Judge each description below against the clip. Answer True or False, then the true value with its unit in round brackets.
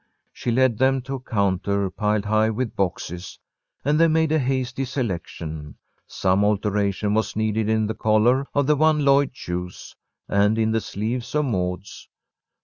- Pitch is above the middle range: False (110 Hz)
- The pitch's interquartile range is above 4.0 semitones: True (4.7 semitones)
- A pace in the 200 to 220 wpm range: False (160 wpm)